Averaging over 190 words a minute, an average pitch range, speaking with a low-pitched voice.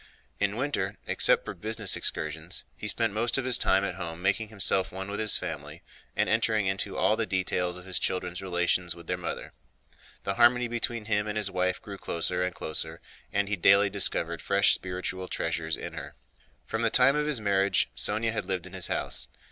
Yes: average, 200 wpm; average, 3.2 semitones; very low, 95 Hz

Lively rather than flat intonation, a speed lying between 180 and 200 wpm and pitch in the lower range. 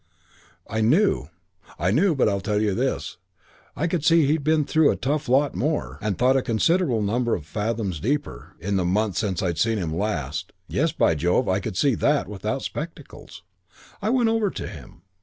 Yes: wide, 7.1 semitones; average, 195 wpm; low, 115 Hz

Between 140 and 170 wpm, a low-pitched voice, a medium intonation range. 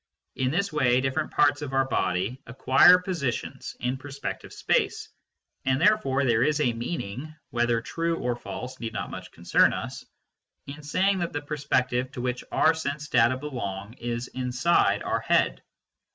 Yes: average, 160 wpm; low, 130 Hz; average, 3.7 semitones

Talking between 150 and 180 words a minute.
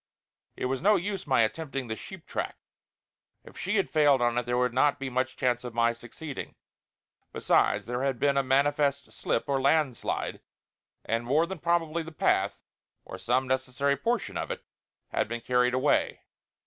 Yes: average, 175 wpm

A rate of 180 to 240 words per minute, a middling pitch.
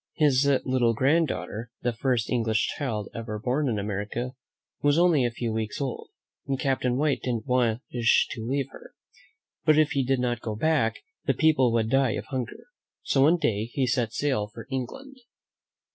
No: average, 185 wpm; low, 125 Hz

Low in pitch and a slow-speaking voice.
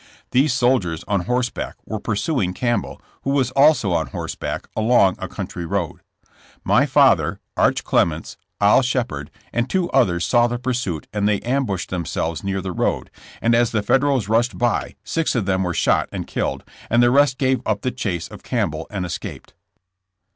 No: low, 115 Hz; average, 185 wpm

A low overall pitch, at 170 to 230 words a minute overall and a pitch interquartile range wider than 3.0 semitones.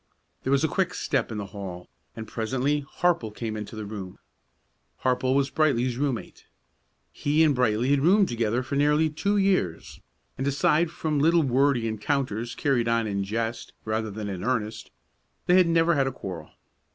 Yes: low, 125 Hz; average, 175 wpm; average, 5.2 semitones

